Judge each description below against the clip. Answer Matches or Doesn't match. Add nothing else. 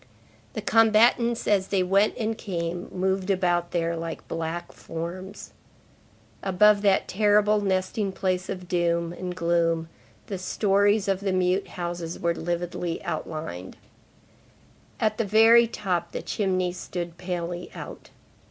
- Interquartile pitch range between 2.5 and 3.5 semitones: Matches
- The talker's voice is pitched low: Doesn't match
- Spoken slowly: Matches